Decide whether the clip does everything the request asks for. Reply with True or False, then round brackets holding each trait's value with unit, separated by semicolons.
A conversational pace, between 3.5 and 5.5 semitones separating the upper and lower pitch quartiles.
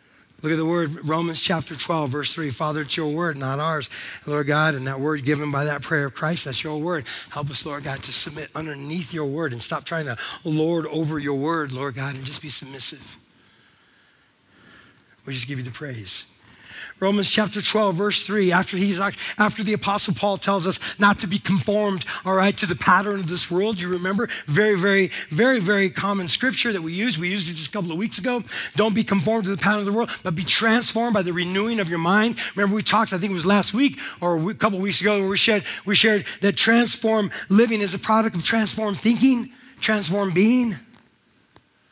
False (215 wpm; 5.0 semitones)